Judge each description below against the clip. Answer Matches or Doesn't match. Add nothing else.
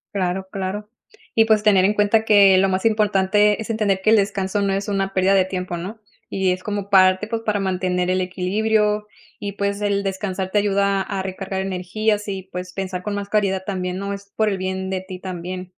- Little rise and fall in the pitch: Matches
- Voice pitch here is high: Matches